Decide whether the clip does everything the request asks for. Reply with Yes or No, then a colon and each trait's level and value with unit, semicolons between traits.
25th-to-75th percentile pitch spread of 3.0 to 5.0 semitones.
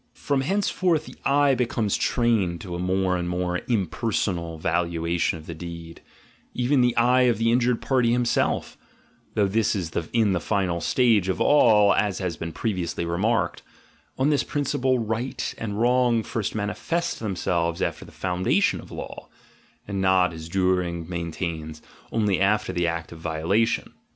No: wide, 5.5 semitones